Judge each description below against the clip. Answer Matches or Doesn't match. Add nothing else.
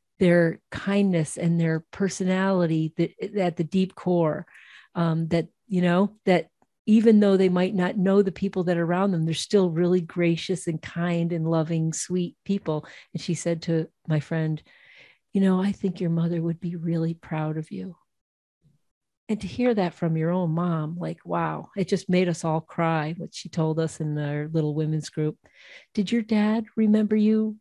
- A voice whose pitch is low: Doesn't match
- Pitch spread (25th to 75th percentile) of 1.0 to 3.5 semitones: Matches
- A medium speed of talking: Matches